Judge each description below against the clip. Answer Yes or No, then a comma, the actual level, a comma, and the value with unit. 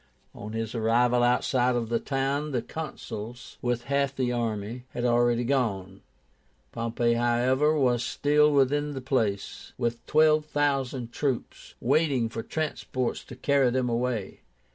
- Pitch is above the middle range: No, low, 125 Hz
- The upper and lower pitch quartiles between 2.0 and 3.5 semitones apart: Yes, average, 2.8 semitones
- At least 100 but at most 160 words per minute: Yes, average, 140 wpm